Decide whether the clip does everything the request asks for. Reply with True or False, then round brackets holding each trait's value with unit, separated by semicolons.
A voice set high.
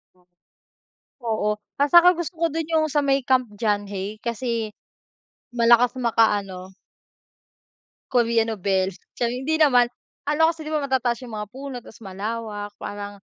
True (235 Hz)